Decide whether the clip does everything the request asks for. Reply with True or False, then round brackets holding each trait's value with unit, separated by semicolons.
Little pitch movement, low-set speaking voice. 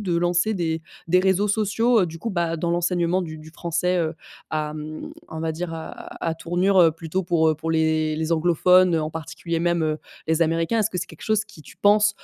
False (2.3 semitones; 170 Hz)